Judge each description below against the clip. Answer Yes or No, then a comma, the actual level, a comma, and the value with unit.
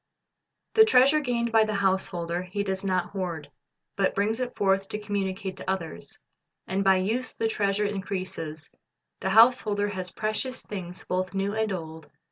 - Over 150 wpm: Yes, average, 160 wpm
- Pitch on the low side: No, high, 195 Hz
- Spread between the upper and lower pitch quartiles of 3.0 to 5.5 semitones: No, narrow, 2.5 semitones